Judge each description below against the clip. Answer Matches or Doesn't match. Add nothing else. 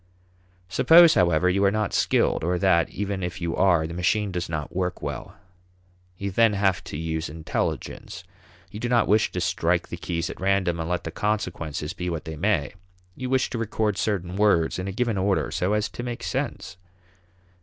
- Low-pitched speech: Matches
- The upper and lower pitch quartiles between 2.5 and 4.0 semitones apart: Matches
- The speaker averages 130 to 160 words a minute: Doesn't match